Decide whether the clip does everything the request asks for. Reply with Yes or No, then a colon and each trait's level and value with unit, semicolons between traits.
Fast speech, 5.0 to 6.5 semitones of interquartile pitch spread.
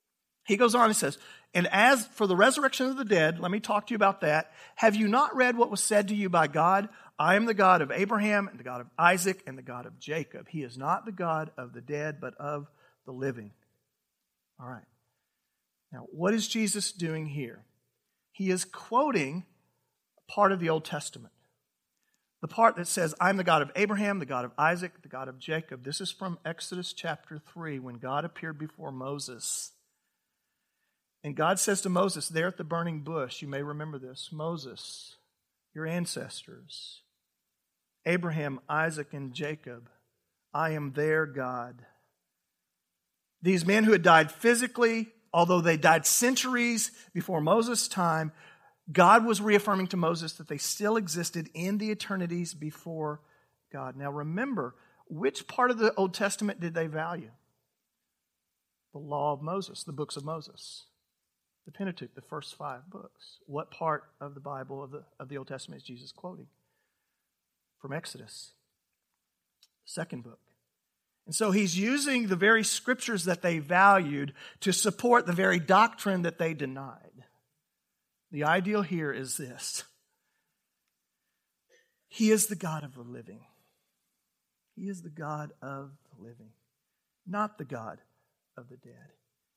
No: average, 160 wpm; wide, 5.4 semitones